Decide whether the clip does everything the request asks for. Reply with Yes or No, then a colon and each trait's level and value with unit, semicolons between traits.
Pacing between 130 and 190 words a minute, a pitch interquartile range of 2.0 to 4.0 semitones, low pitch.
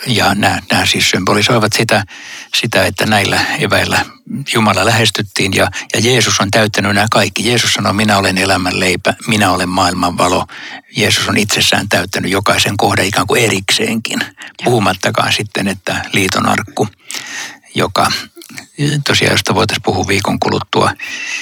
Yes: average, 135 wpm; average, 2.7 semitones; low, 105 Hz